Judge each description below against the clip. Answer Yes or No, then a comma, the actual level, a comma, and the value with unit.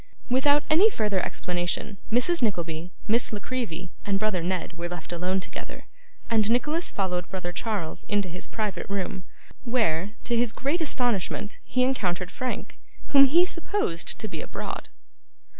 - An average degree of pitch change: No, wide, 5.8 semitones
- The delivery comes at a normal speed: Yes, average, 150 wpm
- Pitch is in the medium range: No, high, 210 Hz